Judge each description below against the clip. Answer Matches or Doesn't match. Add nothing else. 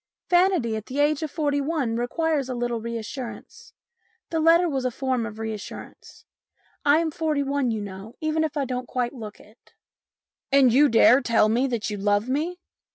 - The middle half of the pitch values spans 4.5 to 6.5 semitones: Matches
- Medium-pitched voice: Doesn't match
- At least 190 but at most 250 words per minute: Matches